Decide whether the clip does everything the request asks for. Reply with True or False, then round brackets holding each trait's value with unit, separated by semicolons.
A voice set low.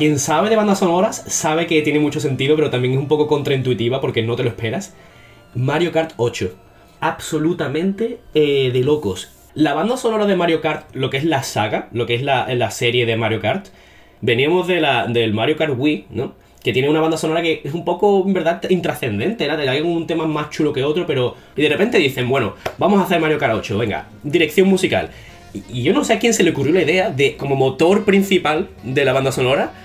False (150 Hz)